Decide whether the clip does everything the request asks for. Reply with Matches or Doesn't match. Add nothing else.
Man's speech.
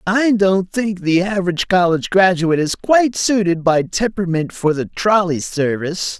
Matches